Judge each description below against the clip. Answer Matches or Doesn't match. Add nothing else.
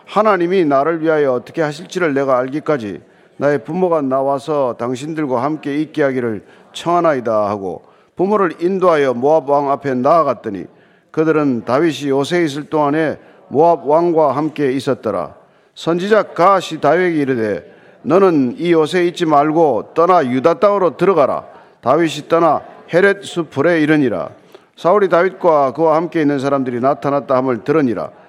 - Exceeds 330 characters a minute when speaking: Matches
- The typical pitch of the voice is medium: Matches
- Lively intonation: Doesn't match